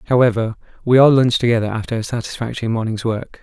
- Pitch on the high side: No, low, 115 Hz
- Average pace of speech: Yes, average, 175 wpm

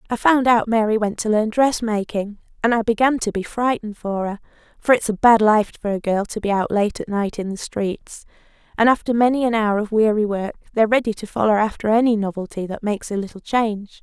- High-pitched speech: Yes, high, 215 Hz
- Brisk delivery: Yes, fast, 230 wpm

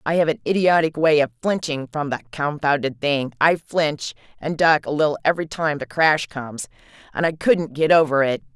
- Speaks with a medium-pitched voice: Yes, medium, 150 Hz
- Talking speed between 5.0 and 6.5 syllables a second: Yes, 5.3 syllables/s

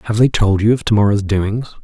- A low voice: Yes, low, 105 Hz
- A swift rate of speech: Yes, fast, 260 wpm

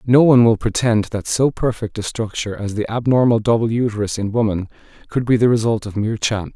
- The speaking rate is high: Yes, fast, 210 wpm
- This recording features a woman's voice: No, male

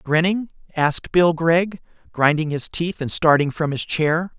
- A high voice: No, medium, 160 Hz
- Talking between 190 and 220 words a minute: No, average, 165 wpm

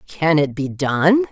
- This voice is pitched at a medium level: Yes, medium, 165 Hz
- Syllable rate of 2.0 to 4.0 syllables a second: Yes, 3.5 syllables/s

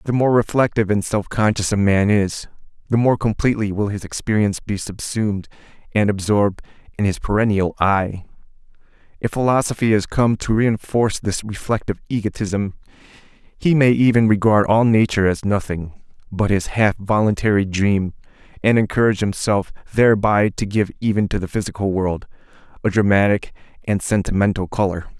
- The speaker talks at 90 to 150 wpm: Yes, average, 145 wpm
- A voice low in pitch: Yes, low, 105 Hz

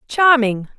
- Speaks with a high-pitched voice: Yes, very high, 255 Hz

